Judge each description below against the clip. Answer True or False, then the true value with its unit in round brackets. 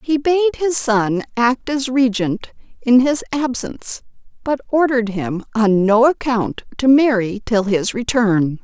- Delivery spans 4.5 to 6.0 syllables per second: False (4.0 syllables/s)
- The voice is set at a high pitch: True (240 Hz)